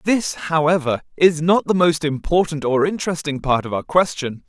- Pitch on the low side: No, medium, 160 Hz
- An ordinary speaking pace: Yes, average, 175 wpm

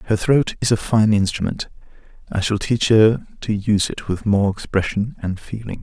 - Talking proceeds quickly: No, average, 185 wpm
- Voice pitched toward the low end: Yes, low, 105 Hz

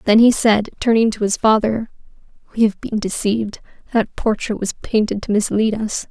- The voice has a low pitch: No, high, 215 Hz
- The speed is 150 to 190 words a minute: Yes, average, 175 wpm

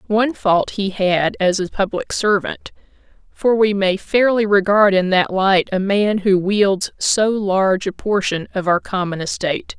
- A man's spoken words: No, female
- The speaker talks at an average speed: Yes, average, 165 wpm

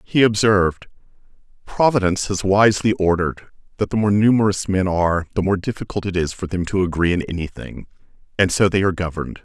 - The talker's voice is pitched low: Yes, very low, 95 Hz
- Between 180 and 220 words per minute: Yes, average, 185 wpm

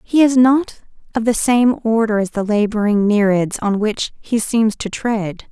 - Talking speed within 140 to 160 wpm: No, average, 185 wpm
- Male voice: No, female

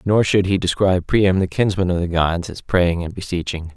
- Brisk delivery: Yes, fast, 225 wpm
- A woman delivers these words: No, male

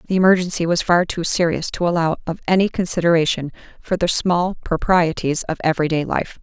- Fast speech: No, average, 175 wpm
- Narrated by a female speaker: Yes, female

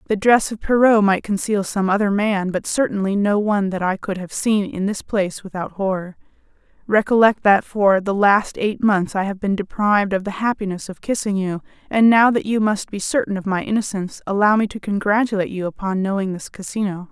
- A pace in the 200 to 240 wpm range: Yes, fast, 205 wpm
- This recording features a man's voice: No, female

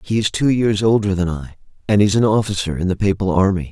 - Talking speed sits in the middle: No, fast, 240 wpm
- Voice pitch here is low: Yes, low, 100 Hz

